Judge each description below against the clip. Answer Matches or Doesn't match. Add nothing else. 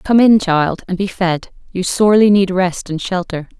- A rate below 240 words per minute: Matches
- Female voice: Matches